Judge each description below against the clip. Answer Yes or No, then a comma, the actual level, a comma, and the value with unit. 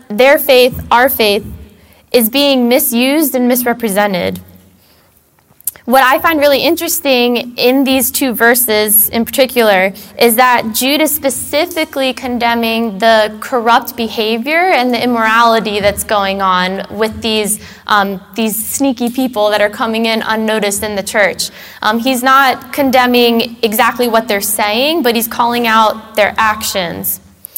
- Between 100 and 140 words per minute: Yes, slow, 135 wpm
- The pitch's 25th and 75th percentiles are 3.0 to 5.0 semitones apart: Yes, average, 3.5 semitones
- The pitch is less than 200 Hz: No, high, 230 Hz